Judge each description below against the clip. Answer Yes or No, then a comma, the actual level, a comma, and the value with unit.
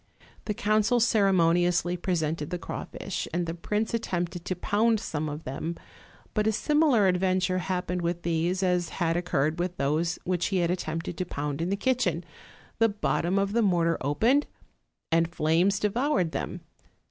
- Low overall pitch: No, medium, 180 Hz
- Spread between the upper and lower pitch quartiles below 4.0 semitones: Yes, average, 3.4 semitones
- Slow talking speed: No, average, 165 wpm